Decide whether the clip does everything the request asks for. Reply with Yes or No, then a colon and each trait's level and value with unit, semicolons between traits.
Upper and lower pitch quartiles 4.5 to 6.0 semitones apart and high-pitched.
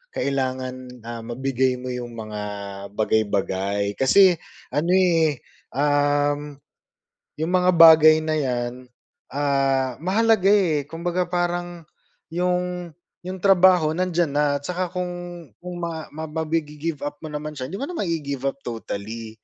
No: average, 5.0 semitones; medium, 150 Hz